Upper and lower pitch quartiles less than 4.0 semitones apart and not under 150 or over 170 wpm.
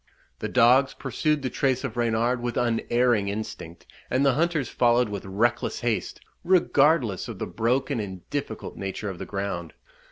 No: average, 4.4 semitones; average, 160 wpm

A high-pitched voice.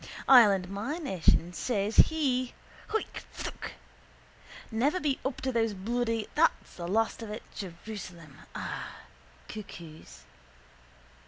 Yes: high, 220 Hz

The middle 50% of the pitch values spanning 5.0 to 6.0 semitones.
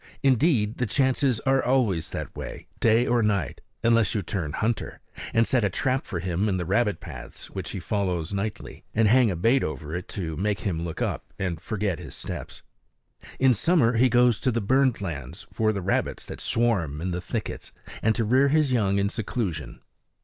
Yes: average, 5.3 semitones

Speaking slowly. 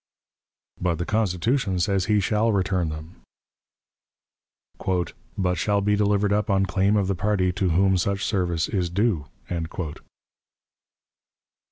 Yes: slow, 125 wpm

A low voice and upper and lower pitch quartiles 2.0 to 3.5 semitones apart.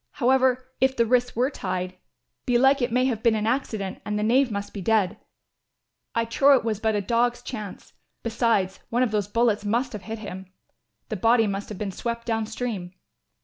No: high, 225 Hz; average, 3.0 semitones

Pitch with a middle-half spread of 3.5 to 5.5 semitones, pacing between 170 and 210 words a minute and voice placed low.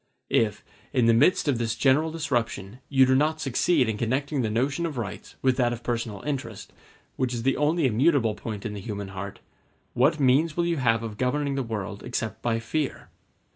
Yes: average, 4.2 semitones; average, 200 wpm; low, 125 Hz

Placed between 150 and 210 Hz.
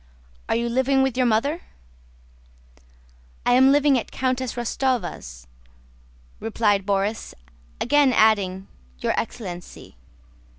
No: high, 235 Hz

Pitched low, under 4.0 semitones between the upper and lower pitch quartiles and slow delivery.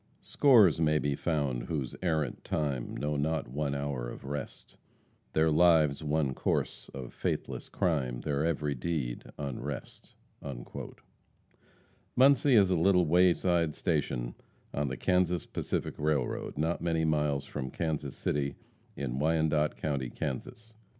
Yes: very low, 75 Hz; average, 3.1 semitones; slow, 130 wpm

